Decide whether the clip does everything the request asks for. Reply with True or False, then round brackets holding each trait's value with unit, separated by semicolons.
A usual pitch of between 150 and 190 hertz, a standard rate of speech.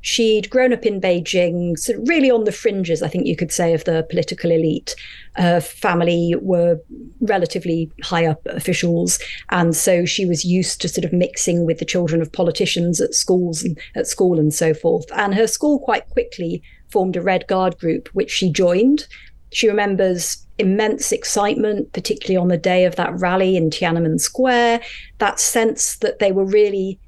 True (185 Hz; 180 wpm)